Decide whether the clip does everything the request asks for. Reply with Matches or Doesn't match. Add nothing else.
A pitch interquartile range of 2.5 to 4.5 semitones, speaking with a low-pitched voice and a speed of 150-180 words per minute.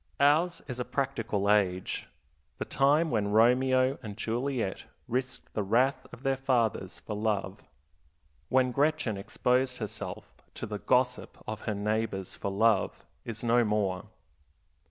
Doesn't match